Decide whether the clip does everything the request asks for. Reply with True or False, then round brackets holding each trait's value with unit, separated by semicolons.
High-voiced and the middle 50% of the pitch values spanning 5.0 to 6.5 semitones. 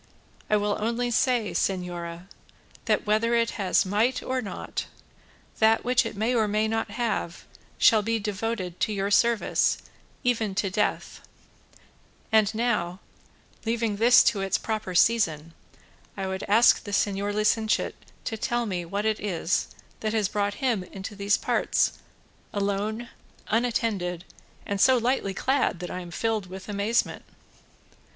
False (210 Hz; 2.9 semitones)